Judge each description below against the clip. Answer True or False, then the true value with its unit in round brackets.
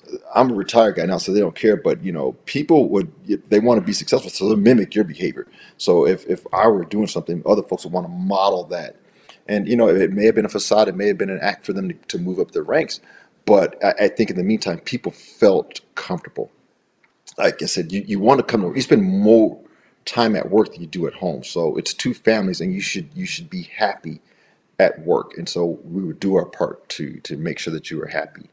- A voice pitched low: False (165 Hz)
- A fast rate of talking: True (250 wpm)